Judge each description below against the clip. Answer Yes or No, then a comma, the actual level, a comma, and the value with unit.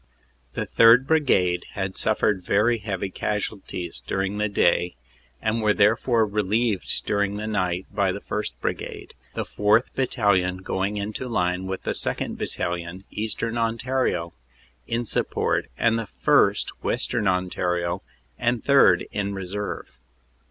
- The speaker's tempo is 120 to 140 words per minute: Yes, slow, 135 wpm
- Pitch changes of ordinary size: Yes, average, 3.4 semitones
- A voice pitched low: Yes, low, 105 Hz